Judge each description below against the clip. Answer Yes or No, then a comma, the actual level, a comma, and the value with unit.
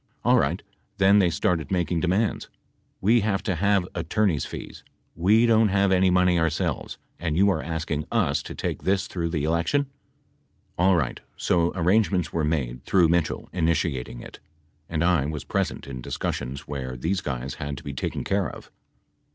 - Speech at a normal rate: Yes, average, 165 wpm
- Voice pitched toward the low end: Yes, very low, 85 Hz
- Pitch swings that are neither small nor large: Yes, average, 4.0 semitones